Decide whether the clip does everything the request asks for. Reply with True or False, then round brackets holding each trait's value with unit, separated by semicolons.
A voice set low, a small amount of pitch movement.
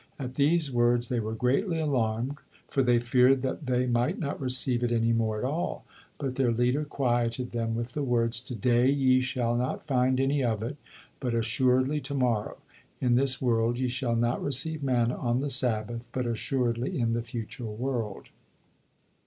True (125 Hz; 2.3 semitones)